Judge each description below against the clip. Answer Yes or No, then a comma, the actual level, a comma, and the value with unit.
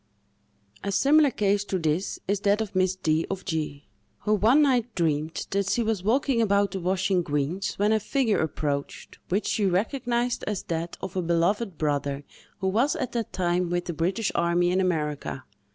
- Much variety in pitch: No, average, 4.2 semitones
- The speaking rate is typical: Yes, average, 185 wpm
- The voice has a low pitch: No, high, 190 Hz